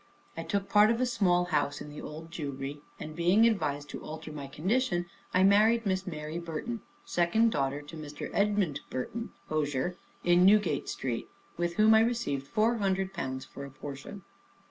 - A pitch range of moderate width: No, wide, 6.1 semitones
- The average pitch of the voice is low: No, medium, 175 Hz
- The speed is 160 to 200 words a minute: Yes, average, 175 wpm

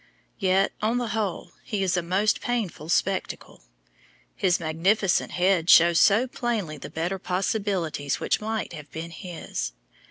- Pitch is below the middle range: No, high, 190 Hz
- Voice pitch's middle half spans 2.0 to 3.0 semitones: No, average, 4.0 semitones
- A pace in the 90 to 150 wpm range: Yes, average, 145 wpm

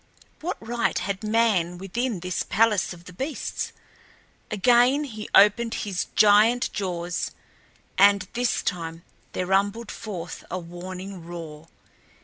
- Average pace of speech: No, slow, 125 wpm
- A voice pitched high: Yes, high, 200 Hz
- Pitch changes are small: No, average, 4.3 semitones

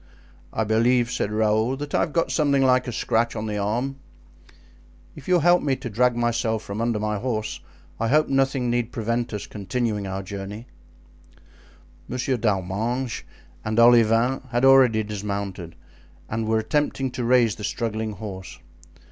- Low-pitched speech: Yes, low, 115 Hz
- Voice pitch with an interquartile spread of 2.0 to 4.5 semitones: Yes, average, 3.1 semitones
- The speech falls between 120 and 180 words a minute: Yes, average, 160 wpm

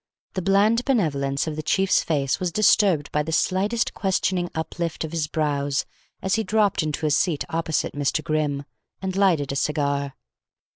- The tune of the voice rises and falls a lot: No, average, 4.7 semitones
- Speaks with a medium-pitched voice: Yes, medium, 160 Hz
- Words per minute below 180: Yes, average, 165 wpm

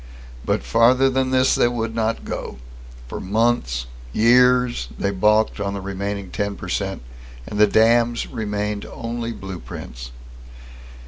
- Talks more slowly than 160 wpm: Yes, slow, 135 wpm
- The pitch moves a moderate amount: Yes, average, 3.2 semitones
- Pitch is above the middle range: No, low, 110 Hz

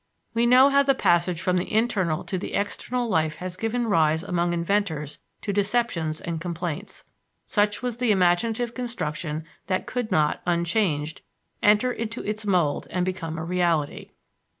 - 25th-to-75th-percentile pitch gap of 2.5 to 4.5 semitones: No, average, 5.1 semitones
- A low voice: No, medium, 185 Hz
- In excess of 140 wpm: Yes, average, 155 wpm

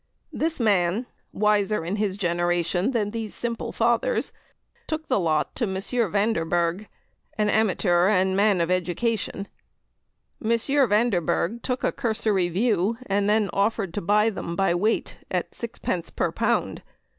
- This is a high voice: Yes, high, 205 Hz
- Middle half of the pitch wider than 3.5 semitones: Yes, average, 3.9 semitones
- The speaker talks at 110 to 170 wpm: Yes, average, 140 wpm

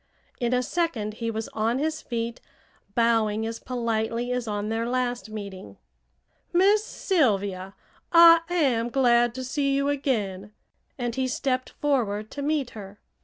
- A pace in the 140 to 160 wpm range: Yes, average, 145 wpm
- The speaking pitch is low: No, high, 240 Hz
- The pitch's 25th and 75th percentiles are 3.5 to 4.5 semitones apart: Yes, average, 3.9 semitones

